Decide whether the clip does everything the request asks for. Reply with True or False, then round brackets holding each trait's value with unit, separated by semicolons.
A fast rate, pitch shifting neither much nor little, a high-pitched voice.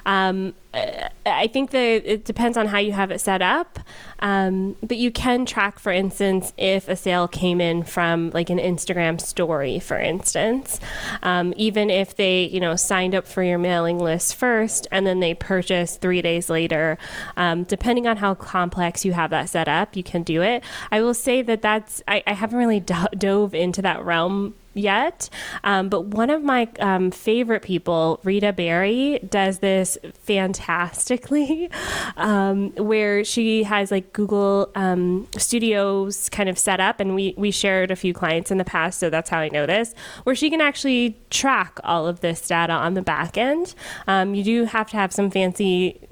False (185 wpm; 3.4 semitones; 195 Hz)